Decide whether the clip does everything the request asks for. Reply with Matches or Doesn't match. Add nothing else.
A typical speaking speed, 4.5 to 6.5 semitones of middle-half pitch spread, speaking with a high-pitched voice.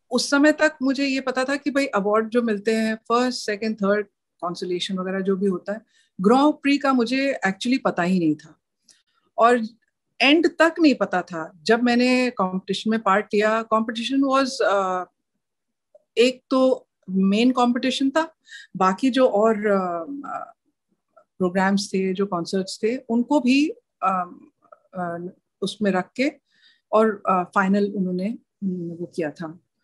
Matches